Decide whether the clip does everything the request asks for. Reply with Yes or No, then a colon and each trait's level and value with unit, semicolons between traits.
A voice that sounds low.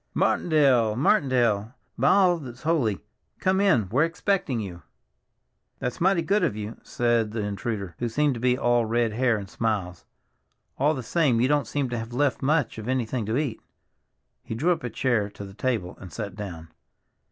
Yes: low, 120 Hz